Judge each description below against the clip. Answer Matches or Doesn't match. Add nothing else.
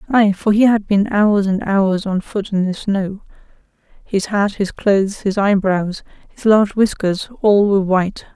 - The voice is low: Doesn't match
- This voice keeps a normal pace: Matches